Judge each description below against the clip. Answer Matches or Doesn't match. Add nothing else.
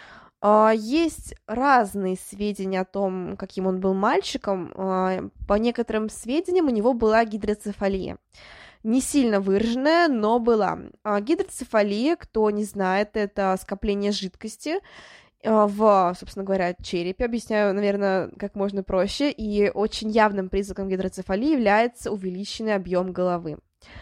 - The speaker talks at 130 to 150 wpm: Doesn't match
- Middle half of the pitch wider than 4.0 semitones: Doesn't match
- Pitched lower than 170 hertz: Doesn't match